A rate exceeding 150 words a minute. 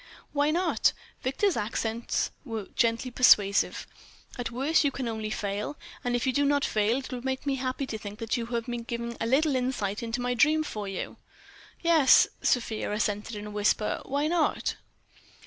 Yes: average, 180 wpm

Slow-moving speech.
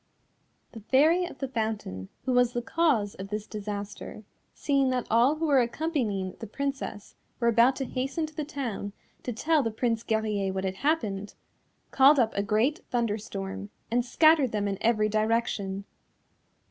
No: average, 165 wpm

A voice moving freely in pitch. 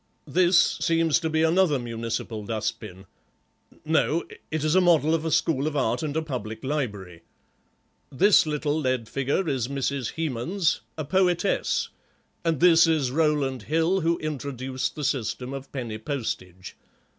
No: average, 4.5 semitones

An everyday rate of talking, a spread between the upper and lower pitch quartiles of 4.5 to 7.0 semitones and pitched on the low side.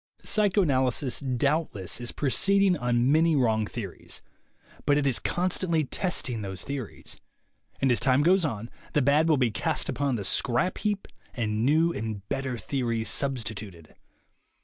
Yes: average, 145 wpm; average, 5.3 semitones; low, 130 Hz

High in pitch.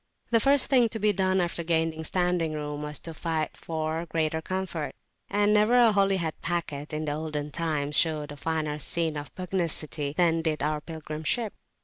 No: medium, 160 Hz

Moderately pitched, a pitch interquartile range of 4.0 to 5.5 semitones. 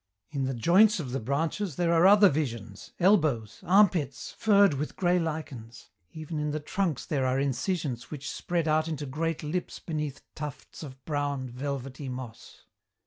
Yes: medium, 150 Hz; average, 4.3 semitones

